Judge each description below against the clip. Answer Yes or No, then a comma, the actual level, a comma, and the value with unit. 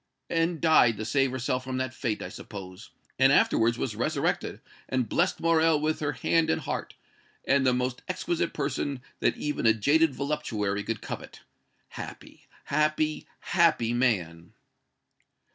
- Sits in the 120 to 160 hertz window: Yes, low, 135 Hz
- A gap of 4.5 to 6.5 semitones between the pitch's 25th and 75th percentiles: Yes, average, 5.1 semitones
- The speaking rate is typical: Yes, average, 145 wpm